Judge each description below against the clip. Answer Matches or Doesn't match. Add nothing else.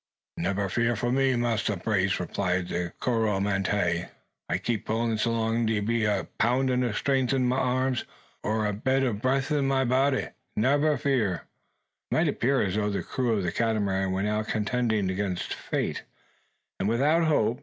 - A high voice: Doesn't match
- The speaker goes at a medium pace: Matches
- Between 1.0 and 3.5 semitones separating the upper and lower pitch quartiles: Doesn't match